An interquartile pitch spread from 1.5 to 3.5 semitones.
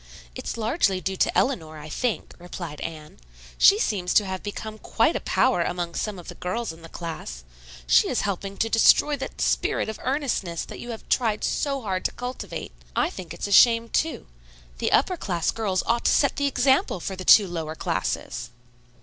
No: wide, 5.6 semitones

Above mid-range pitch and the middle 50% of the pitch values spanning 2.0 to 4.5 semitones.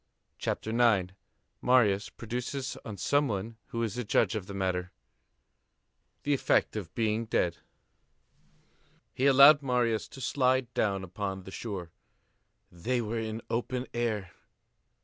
No: low, 115 Hz; average, 4.2 semitones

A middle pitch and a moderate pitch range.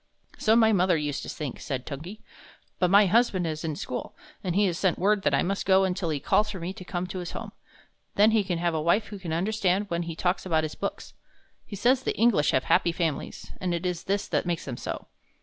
Yes: medium, 180 Hz; average, 3.3 semitones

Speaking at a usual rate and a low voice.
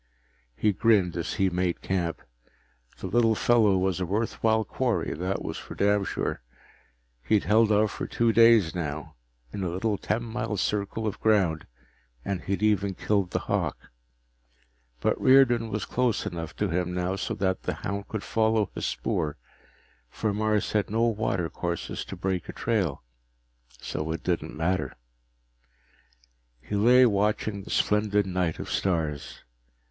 Yes: average, 150 wpm; low, 100 Hz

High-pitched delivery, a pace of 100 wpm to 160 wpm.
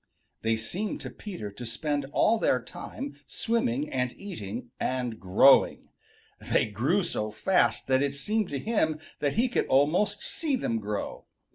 No: medium, 140 Hz; average, 155 wpm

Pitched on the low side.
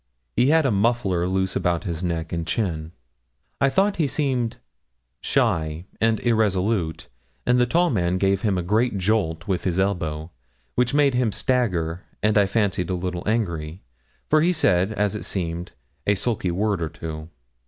Yes: very low, 95 Hz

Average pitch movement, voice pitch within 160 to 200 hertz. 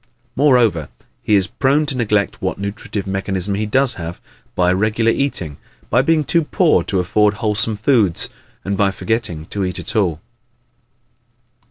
No: average, 4.1 semitones; low, 105 Hz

